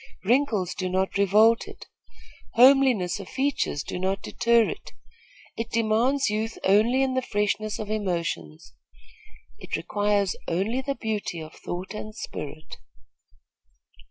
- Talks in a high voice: Yes, high, 210 Hz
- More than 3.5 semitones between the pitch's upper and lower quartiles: Yes, average, 3.9 semitones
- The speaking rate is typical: No, slow, 130 wpm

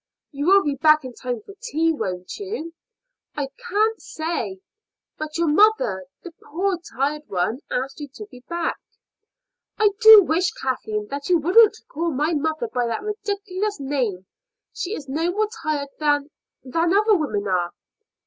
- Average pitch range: No, wide, 6.2 semitones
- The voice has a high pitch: Yes, very high, 310 Hz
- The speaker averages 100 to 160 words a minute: Yes, average, 155 wpm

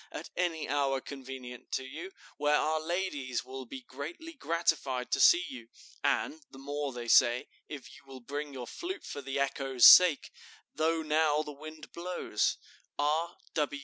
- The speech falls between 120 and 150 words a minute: No, average, 160 wpm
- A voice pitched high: No, medium, 145 Hz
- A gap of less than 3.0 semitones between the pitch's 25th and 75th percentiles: No, average, 3.3 semitones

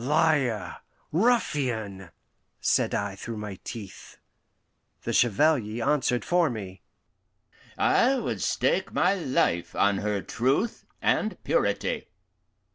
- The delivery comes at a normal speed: No, slow, 105 wpm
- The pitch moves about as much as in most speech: No, wide, 7.6 semitones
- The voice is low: Yes, low, 120 Hz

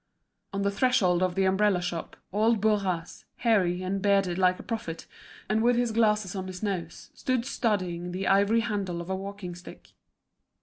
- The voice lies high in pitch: Yes, high, 195 Hz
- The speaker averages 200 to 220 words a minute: No, average, 175 wpm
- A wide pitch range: No, average, 3.0 semitones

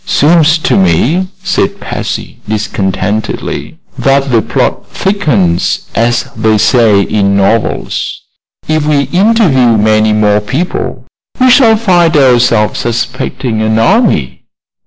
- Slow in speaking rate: Yes, slow, 115 wpm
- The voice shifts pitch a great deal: Yes, wide, 7.9 semitones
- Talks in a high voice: No, low, 120 Hz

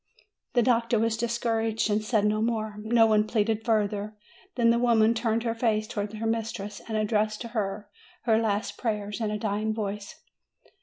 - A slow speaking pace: No, average, 175 wpm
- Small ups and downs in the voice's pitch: Yes, narrow, 1.4 semitones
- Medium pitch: No, high, 220 Hz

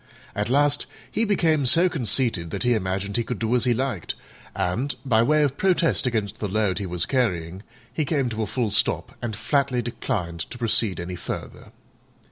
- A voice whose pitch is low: Yes, low, 115 Hz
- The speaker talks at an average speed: Yes, average, 190 wpm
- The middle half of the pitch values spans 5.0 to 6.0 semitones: Yes, average, 5.3 semitones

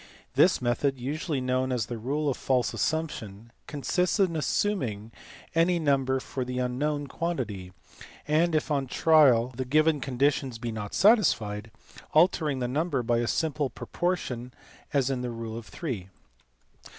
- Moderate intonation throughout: Yes, average, 4.3 semitones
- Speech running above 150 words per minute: No, average, 145 wpm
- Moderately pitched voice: No, low, 130 Hz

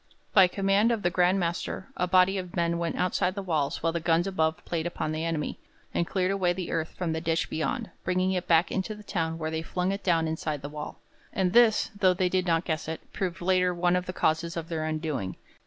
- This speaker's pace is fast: Yes, fast, 235 wpm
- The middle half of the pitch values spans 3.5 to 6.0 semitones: No, narrow, 2.4 semitones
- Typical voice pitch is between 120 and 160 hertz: No, medium, 175 Hz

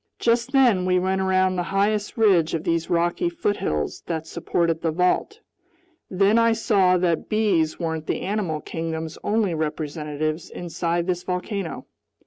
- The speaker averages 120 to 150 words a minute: Yes, average, 145 wpm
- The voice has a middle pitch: Yes, medium, 180 Hz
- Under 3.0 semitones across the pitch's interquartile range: No, average, 3.9 semitones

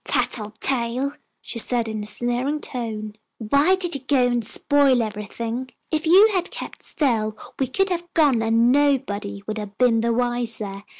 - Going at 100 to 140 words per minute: No, average, 165 wpm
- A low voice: No, high, 240 Hz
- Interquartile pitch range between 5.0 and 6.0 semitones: No, average, 4.4 semitones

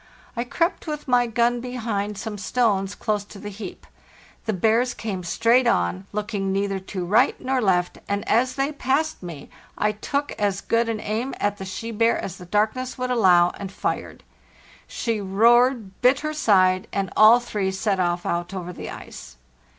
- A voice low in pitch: No, high, 210 Hz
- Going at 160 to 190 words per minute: Yes, average, 180 wpm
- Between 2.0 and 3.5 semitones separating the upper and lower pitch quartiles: No, average, 4.1 semitones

